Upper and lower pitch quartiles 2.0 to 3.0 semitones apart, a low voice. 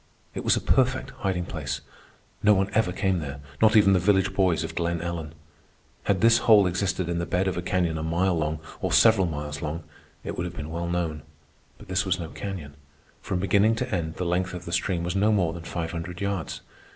Yes: average, 2.7 semitones; very low, 90 Hz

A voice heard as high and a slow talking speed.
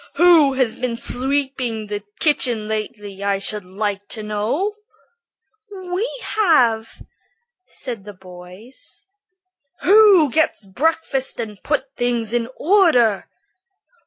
Yes: high, 240 Hz; slow, 105 wpm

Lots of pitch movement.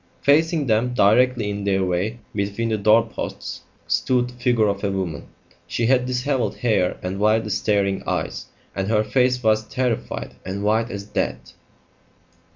No: average, 3.6 semitones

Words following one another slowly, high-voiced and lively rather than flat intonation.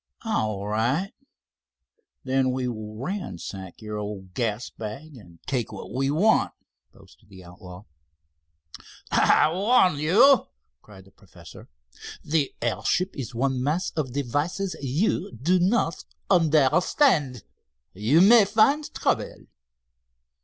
No: slow, 115 wpm; low, 135 Hz; wide, 8.9 semitones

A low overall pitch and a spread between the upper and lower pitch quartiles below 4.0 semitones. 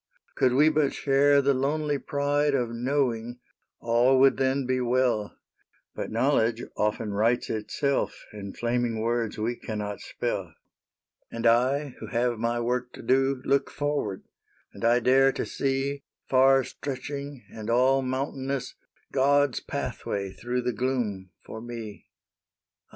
Yes: low, 125 Hz; average, 2.8 semitones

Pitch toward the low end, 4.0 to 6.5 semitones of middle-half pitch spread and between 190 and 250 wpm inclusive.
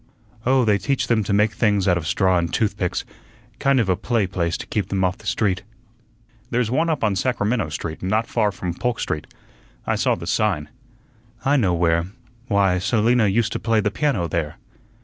Yes: low, 105 Hz; average, 4.3 semitones; average, 195 wpm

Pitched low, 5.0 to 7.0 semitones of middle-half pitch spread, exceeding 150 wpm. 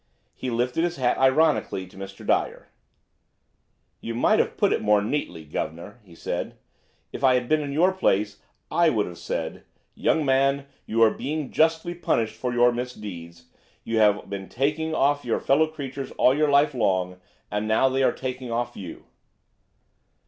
Yes: low, 125 Hz; wide, 5.4 semitones; average, 170 wpm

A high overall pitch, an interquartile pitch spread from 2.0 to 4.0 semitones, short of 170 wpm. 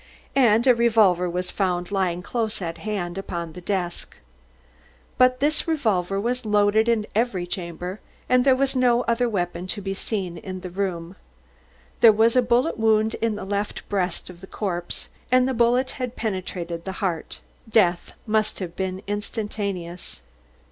No: high, 205 Hz; average, 4.4 semitones; average, 160 wpm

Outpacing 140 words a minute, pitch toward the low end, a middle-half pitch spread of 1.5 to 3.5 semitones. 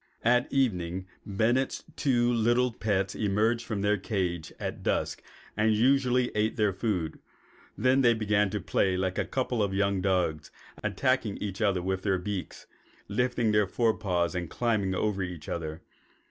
No: average, 160 wpm; low, 105 Hz; average, 4.0 semitones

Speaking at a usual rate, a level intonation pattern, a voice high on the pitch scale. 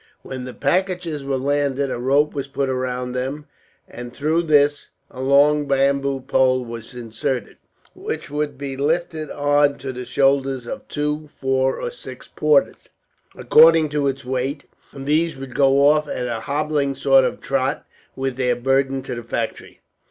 No: average, 165 wpm; narrow, 2.0 semitones; low, 135 Hz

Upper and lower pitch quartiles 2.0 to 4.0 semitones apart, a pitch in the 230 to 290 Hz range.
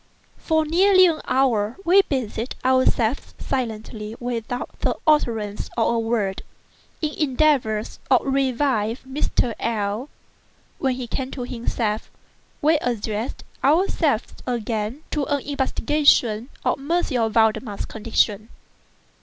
No: average, 4.4 semitones; high, 245 Hz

